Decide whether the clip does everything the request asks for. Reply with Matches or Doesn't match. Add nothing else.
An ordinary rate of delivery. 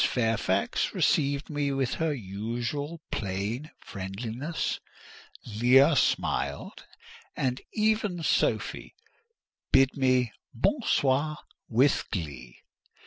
Doesn't match